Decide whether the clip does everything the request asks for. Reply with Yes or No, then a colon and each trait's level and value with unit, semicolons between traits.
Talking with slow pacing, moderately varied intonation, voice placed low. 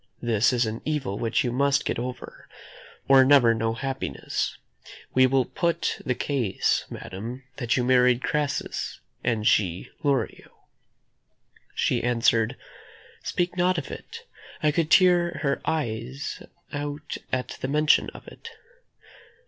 Yes: slow, 130 wpm; average, 3.8 semitones; low, 130 Hz